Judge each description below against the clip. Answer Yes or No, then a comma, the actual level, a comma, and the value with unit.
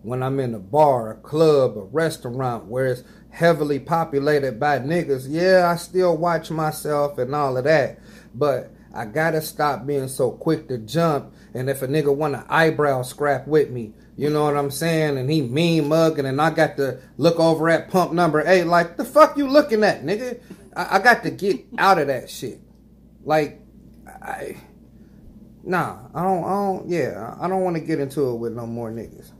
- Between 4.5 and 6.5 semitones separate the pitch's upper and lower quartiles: No, average, 3.8 semitones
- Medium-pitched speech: Yes, medium, 155 Hz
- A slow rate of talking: No, average, 195 wpm